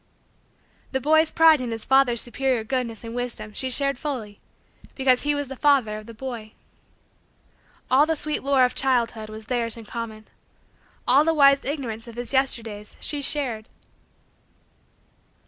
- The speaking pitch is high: Yes, very high, 250 Hz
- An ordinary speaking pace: Yes, average, 155 wpm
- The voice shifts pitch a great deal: No, average, 3.5 semitones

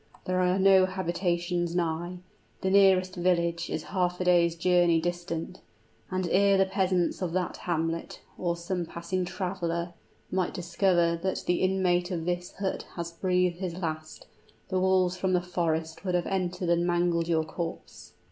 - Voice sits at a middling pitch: Yes, medium, 180 Hz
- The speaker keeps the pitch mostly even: Yes, narrow, 1.4 semitones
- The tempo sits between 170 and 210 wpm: No, average, 160 wpm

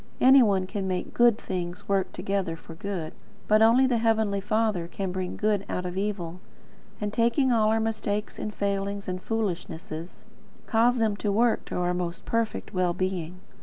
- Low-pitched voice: No, high, 200 Hz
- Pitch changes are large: No, average, 3.4 semitones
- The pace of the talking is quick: No, average, 175 wpm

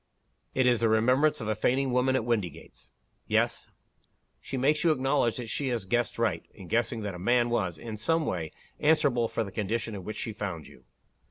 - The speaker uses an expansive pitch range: No, average, 3.4 semitones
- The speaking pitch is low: Yes, low, 115 Hz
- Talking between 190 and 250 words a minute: Yes, average, 200 wpm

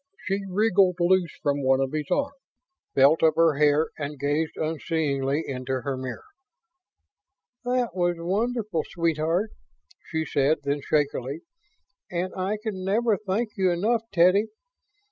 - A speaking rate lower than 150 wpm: Yes, slow, 135 wpm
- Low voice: No, medium, 165 Hz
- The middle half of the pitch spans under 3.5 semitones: No, average, 5.1 semitones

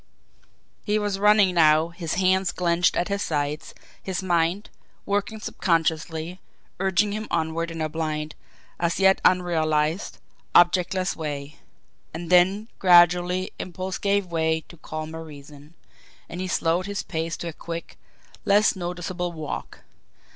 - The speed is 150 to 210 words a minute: No, slow, 135 wpm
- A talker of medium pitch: Yes, medium, 175 Hz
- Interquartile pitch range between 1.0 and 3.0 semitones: Yes, average, 2.7 semitones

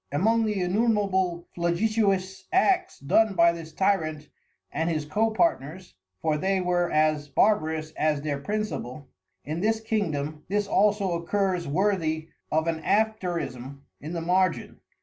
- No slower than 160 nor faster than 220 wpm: No, slow, 135 wpm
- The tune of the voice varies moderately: Yes, average, 4.9 semitones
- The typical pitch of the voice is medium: Yes, medium, 175 Hz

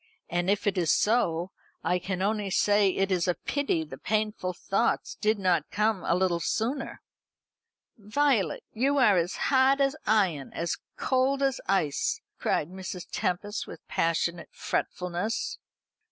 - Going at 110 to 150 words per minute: Yes, average, 145 wpm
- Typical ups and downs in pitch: Yes, average, 3.9 semitones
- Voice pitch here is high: Yes, high, 195 Hz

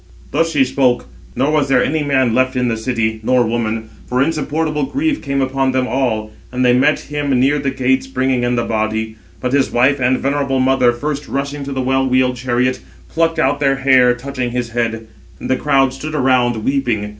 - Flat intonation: Yes, narrow, 2.1 semitones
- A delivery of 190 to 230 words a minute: Yes, average, 200 wpm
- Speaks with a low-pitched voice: Yes, low, 130 Hz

